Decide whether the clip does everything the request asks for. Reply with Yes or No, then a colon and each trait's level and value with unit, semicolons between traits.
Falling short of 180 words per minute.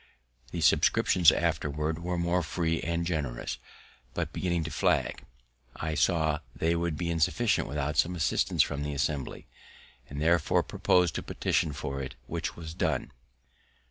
Yes: average, 145 wpm